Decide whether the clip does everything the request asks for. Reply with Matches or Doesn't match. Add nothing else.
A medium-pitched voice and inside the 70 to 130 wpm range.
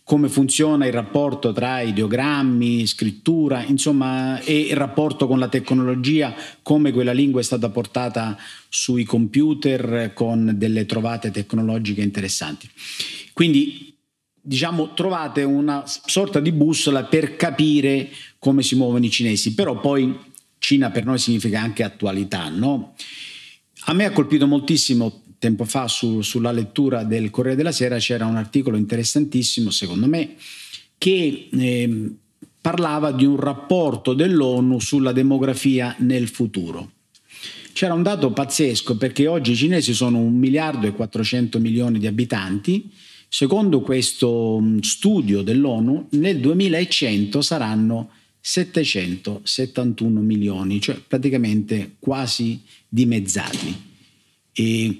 Doesn't match